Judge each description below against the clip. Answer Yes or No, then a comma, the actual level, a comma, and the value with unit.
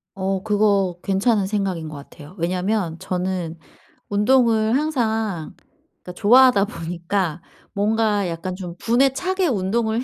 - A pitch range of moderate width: Yes, average, 3.7 semitones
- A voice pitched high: Yes, high, 200 Hz